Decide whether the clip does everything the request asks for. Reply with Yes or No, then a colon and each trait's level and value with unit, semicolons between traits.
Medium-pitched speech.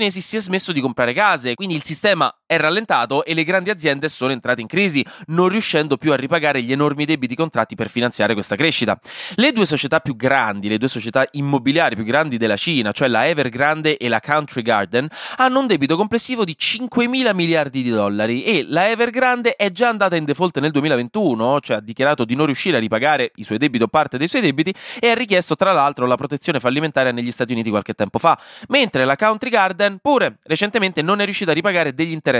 Yes: medium, 155 Hz